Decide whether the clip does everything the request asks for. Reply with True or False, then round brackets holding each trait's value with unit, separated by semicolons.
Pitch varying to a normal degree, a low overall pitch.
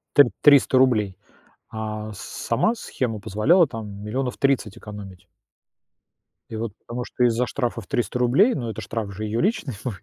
True (3.4 semitones; 115 Hz)